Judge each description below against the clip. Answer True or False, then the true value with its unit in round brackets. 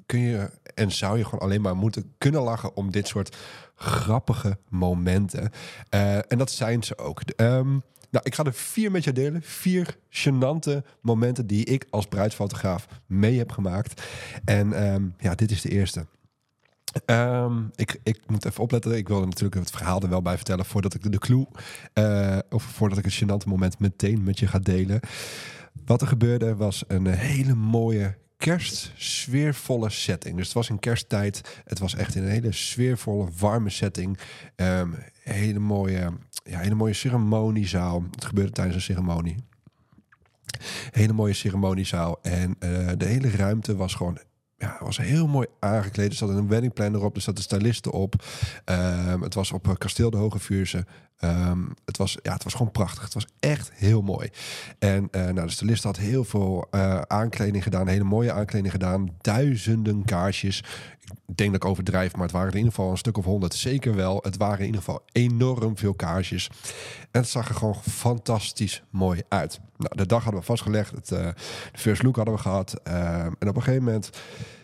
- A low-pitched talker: True (105 Hz)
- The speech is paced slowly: False (185 wpm)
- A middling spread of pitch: True (3.5 semitones)